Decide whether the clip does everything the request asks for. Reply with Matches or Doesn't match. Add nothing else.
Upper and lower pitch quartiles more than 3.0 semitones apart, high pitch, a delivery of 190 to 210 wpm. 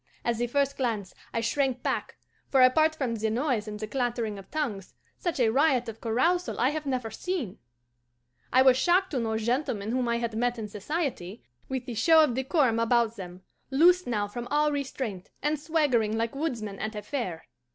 Matches